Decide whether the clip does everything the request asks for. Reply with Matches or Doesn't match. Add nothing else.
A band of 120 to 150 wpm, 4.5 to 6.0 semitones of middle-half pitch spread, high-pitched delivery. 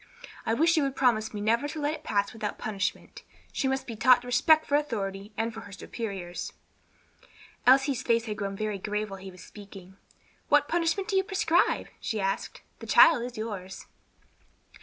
Doesn't match